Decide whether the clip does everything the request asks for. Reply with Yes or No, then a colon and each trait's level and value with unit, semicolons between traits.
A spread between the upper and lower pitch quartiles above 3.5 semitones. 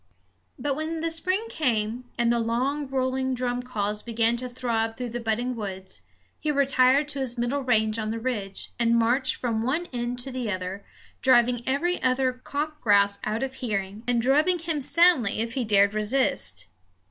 No: average, 3.2 semitones